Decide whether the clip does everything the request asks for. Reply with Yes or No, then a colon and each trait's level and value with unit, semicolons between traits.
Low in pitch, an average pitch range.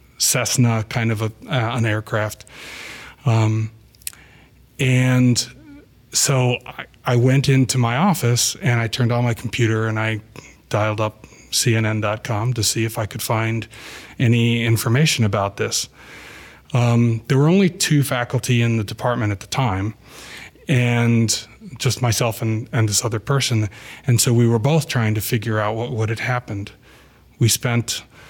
No: low, 120 Hz; narrow, 2.2 semitones